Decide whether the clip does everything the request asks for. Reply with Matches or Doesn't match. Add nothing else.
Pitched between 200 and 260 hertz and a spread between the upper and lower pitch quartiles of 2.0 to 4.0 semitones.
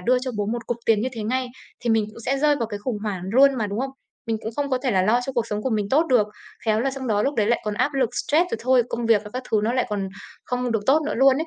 Matches